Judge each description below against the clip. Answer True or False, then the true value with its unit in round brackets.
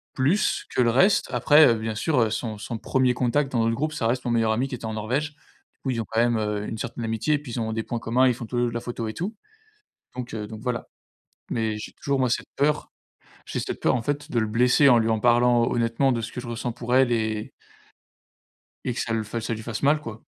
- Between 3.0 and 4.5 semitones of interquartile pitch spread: False (2.6 semitones)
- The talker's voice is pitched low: True (120 Hz)